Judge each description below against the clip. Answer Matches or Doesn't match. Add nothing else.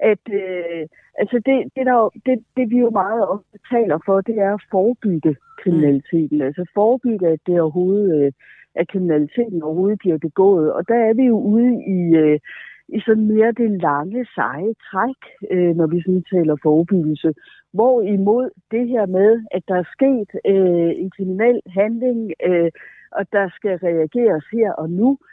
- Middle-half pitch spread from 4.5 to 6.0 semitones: Matches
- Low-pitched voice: Doesn't match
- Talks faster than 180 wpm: Doesn't match